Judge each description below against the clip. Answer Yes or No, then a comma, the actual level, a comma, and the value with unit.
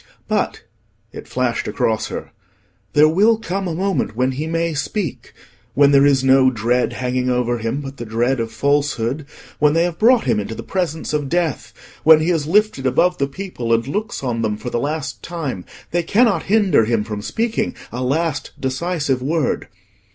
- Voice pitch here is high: No, medium, 140 Hz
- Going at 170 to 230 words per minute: Yes, average, 180 wpm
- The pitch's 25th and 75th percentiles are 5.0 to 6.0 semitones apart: Yes, wide, 5.6 semitones